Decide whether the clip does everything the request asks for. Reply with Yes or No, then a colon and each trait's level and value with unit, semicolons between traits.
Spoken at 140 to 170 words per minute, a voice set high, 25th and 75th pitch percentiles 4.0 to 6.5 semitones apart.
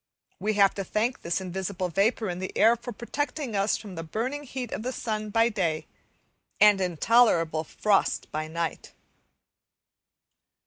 Yes: average, 150 wpm; high, 205 Hz; average, 4.4 semitones